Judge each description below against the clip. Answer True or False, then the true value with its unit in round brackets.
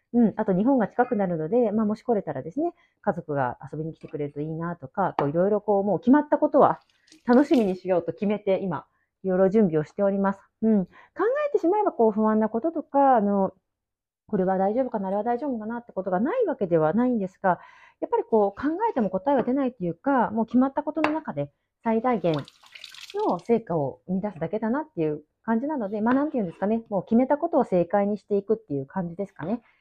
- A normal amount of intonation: False (5.8 semitones)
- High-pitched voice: True (215 Hz)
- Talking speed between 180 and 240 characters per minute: False (455 characters per minute)